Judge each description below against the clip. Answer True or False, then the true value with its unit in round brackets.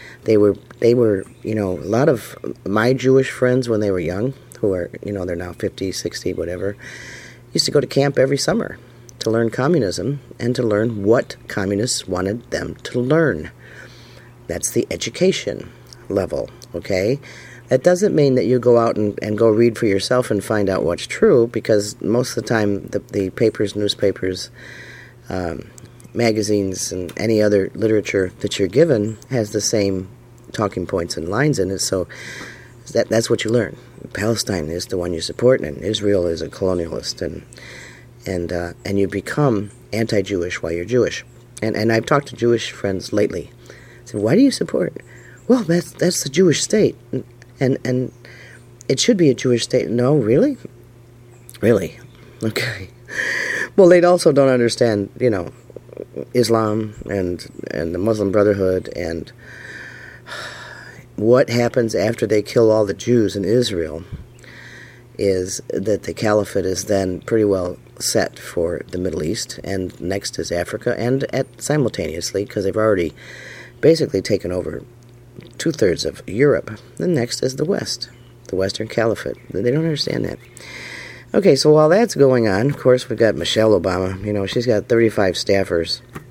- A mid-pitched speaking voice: False (115 Hz)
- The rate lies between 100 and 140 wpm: False (165 wpm)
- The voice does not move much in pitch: False (3.8 semitones)